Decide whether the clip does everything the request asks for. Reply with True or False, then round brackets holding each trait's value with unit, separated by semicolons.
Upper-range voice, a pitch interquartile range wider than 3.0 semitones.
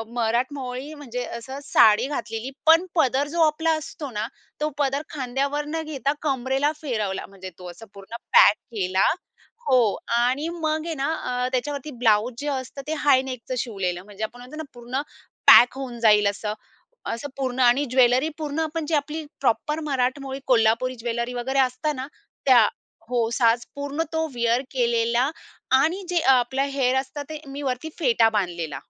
True (255 Hz; 3.6 semitones)